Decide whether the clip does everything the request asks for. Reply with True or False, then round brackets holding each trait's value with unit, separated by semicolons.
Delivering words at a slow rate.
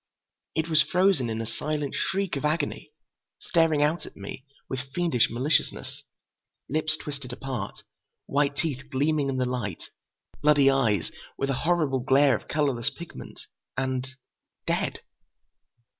True (130 wpm)